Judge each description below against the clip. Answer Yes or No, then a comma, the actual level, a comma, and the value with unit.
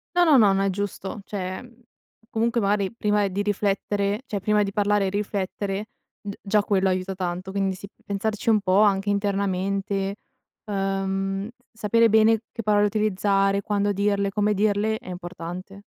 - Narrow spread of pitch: Yes, narrow, 1.3 semitones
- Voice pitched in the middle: No, high, 200 Hz